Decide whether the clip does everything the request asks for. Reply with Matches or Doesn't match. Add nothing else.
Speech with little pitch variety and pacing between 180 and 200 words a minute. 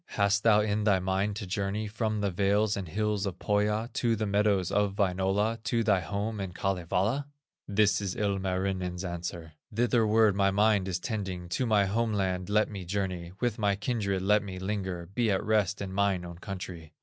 Matches